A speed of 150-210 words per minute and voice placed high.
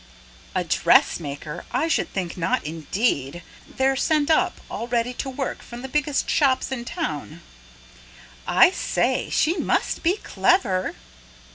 No: slow, 135 wpm; very high, 250 Hz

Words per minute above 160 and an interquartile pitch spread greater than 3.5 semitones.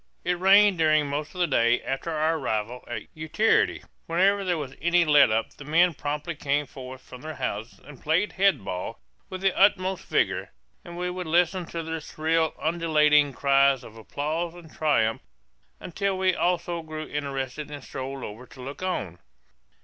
Yes: average, 175 wpm; average, 4.3 semitones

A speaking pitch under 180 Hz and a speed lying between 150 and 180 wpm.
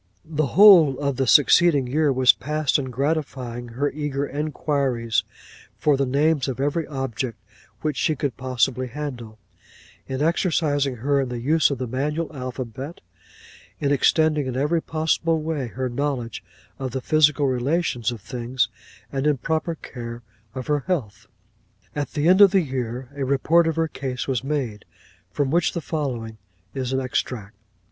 Yes: medium, 140 Hz; average, 160 wpm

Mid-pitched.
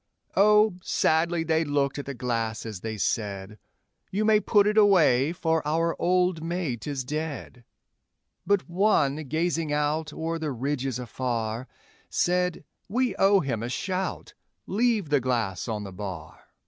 Yes: medium, 150 Hz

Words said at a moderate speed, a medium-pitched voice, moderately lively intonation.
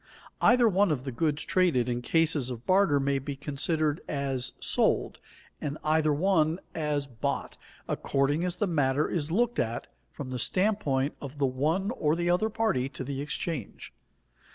Yes: average, 170 wpm; medium, 150 Hz; average, 4.3 semitones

